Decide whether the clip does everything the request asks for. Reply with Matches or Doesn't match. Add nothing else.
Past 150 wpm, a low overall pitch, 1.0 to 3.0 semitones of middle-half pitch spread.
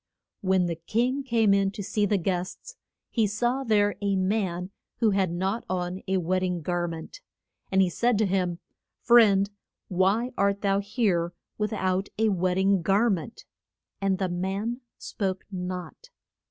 Doesn't match